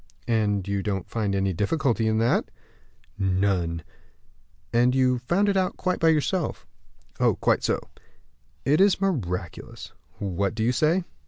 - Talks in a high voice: No, low, 115 Hz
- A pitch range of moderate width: No, wide, 8.0 semitones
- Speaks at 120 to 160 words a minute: Yes, average, 140 wpm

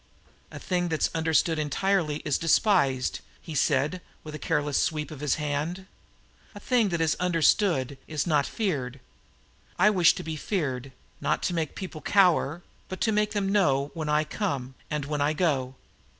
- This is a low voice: No, medium, 155 Hz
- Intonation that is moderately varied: Yes, average, 4.0 semitones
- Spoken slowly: No, average, 170 wpm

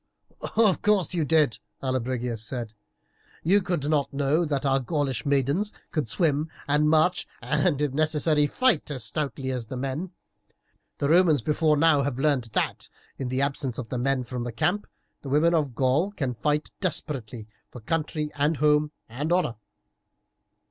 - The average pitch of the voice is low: No, medium, 145 Hz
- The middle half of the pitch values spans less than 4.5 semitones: Yes, average, 3.3 semitones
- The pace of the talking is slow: No, average, 160 wpm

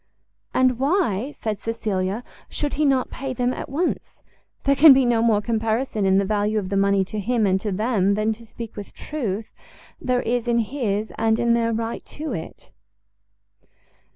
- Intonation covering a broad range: No, average, 3.5 semitones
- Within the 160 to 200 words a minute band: Yes, average, 180 wpm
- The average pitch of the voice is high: Yes, high, 225 Hz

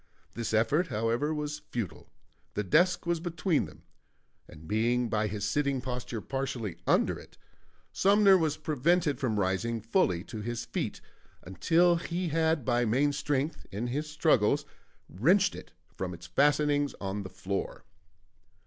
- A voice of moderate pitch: No, low, 130 Hz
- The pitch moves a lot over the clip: Yes, wide, 6.2 semitones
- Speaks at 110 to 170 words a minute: Yes, average, 145 wpm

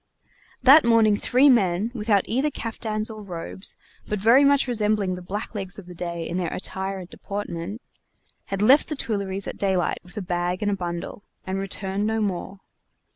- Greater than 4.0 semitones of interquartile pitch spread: No, average, 3.2 semitones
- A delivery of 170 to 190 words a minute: Yes, average, 180 wpm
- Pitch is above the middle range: Yes, high, 200 Hz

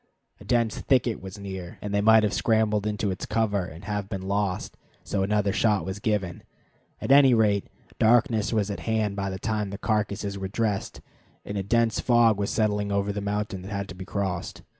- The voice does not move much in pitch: Yes, narrow, 2.0 semitones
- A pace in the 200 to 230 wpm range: Yes, fast, 205 wpm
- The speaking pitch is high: No, low, 105 Hz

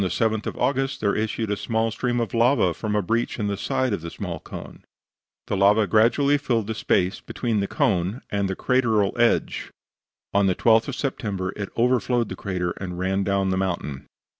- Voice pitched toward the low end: Yes, low, 105 Hz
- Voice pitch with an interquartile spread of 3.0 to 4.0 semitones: Yes, average, 3.6 semitones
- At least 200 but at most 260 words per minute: Yes, fast, 205 wpm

